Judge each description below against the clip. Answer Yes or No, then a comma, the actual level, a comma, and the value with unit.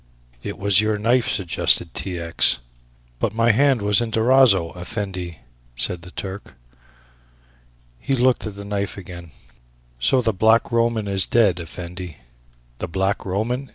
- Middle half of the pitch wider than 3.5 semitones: Yes, average, 4.1 semitones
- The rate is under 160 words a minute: Yes, average, 145 wpm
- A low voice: Yes, low, 100 Hz